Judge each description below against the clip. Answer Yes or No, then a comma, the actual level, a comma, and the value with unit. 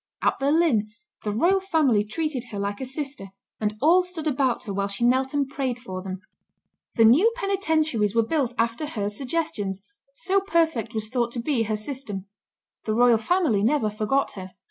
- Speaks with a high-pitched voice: Yes, high, 245 Hz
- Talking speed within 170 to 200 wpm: Yes, average, 180 wpm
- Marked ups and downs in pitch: Yes, wide, 6.4 semitones